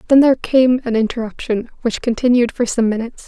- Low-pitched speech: No, high, 235 Hz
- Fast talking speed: No, average, 185 wpm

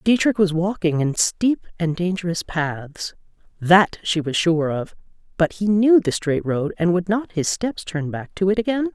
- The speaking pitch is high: No, medium, 180 Hz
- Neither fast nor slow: Yes, average, 195 wpm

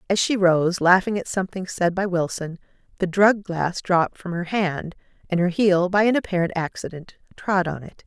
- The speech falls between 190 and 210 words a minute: Yes, average, 195 wpm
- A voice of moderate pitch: Yes, medium, 180 Hz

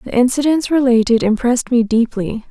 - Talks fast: No, average, 145 wpm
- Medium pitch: No, high, 240 Hz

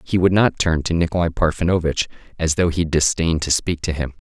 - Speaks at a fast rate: Yes, fast, 210 wpm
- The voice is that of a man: Yes, male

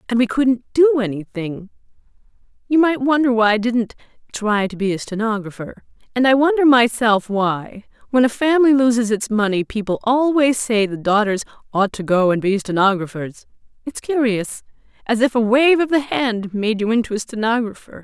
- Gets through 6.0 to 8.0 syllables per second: No, 5.1 syllables/s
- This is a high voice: Yes, high, 230 Hz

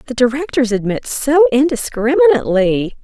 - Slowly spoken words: Yes, slow, 100 wpm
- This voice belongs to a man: No, female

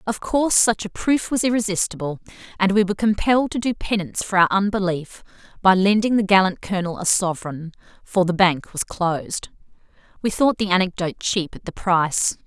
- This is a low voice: No, high, 195 Hz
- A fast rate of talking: No, average, 180 wpm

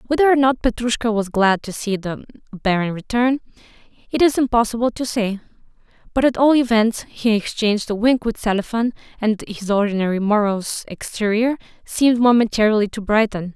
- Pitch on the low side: No, high, 220 Hz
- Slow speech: No, average, 155 wpm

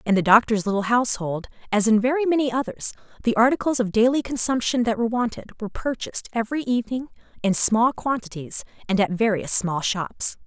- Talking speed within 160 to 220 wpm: Yes, average, 170 wpm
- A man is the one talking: No, female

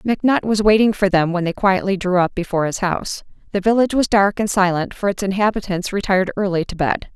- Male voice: No, female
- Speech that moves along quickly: Yes, fast, 220 wpm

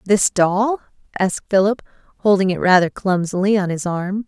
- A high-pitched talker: Yes, high, 195 Hz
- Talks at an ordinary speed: Yes, average, 155 wpm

